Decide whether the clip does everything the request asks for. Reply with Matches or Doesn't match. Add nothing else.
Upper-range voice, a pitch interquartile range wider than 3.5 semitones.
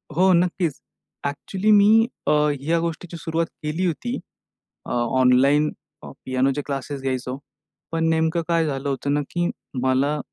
Doesn't match